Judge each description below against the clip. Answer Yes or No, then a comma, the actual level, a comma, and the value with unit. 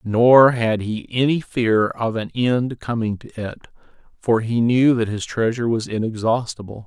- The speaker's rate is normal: Yes, average, 165 wpm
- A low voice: Yes, low, 115 Hz